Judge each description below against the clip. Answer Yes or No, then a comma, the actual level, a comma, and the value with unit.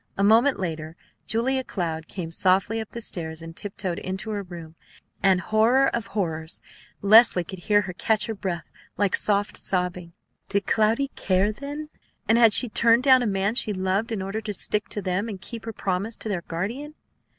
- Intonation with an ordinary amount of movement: Yes, average, 3.7 semitones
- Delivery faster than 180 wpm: Yes, average, 195 wpm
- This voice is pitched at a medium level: No, high, 200 Hz